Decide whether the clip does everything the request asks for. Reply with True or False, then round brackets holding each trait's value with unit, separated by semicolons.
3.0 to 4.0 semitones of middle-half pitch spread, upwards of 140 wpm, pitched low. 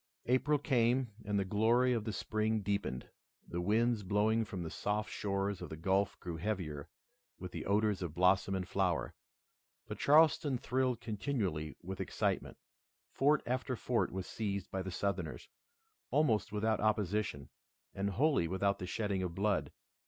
True (3.5 semitones; 155 wpm; 105 Hz)